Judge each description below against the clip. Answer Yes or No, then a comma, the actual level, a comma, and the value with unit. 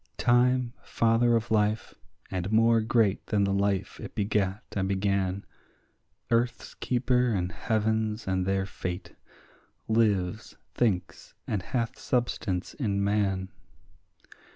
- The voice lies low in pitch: Yes, low, 105 Hz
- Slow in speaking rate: Yes, slow, 115 wpm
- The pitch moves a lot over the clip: No, average, 3.1 semitones